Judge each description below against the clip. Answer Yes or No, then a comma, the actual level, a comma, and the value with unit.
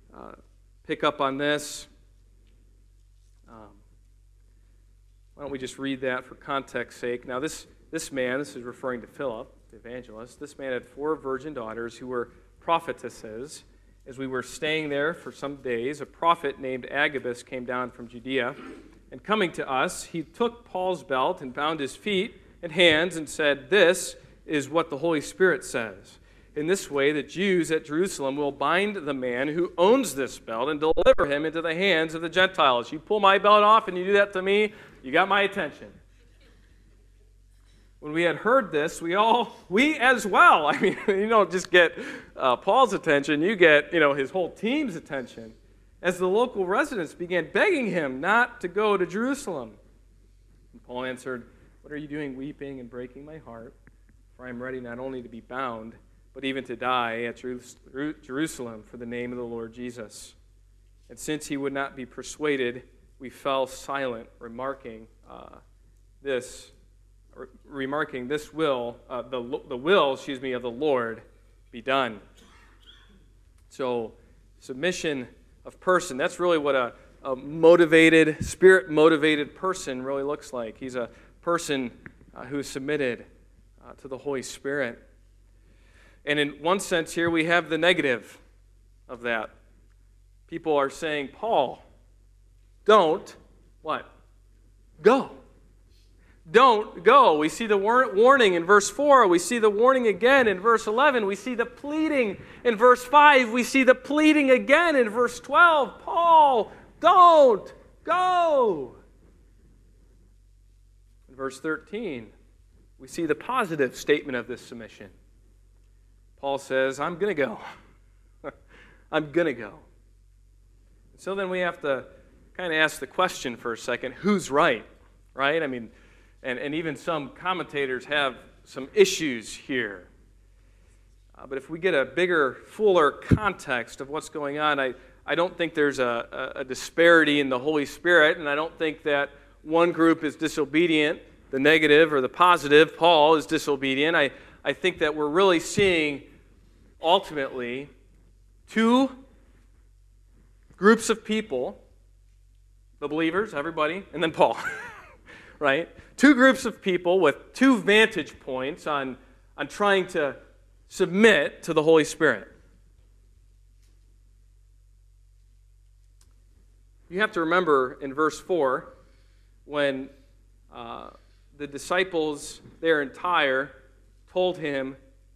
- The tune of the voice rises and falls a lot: Yes, wide, 8.7 semitones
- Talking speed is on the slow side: No, average, 150 wpm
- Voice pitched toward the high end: No, low, 135 Hz